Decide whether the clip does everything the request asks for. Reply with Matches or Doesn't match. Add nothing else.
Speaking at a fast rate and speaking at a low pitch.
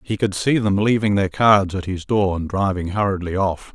Matches